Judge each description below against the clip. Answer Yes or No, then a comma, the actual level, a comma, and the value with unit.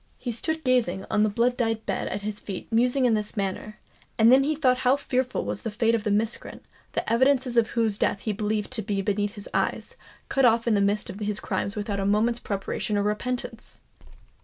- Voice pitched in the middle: No, high, 220 Hz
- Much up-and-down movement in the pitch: No, average, 3.0 semitones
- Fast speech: Yes, fast, 220 wpm